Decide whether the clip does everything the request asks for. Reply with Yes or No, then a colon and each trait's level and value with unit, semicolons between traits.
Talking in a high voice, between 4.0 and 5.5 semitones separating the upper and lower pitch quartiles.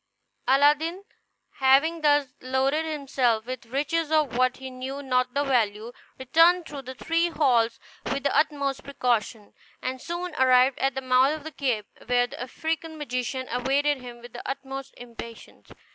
No: very high, 265 Hz; average, 2.9 semitones